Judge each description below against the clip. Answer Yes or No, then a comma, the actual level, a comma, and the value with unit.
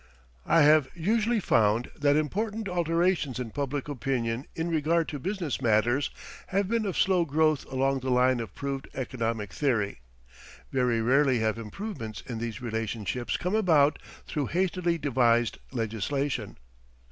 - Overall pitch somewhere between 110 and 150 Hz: Yes, low, 135 Hz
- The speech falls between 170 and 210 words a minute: No, average, 140 wpm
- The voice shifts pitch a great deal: Yes, wide, 6.1 semitones